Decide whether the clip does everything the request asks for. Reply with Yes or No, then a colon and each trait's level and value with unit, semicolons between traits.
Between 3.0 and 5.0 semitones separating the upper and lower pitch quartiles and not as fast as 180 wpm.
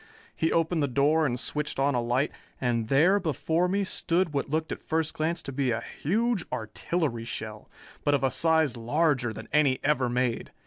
No: average, 4.6 semitones; average, 190 wpm